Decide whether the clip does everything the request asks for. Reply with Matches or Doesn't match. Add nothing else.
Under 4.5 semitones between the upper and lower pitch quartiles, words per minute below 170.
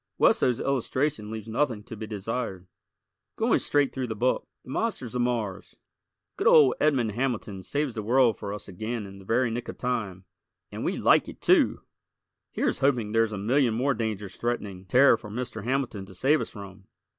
Doesn't match